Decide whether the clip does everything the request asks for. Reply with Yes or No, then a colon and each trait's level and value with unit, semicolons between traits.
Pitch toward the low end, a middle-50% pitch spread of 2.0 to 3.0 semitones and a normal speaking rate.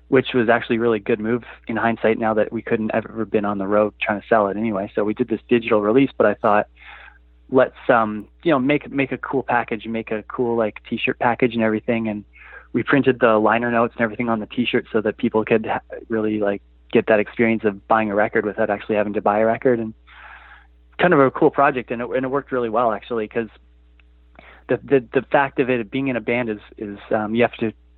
No: low, 115 Hz; narrow, 2.4 semitones; fast, 240 wpm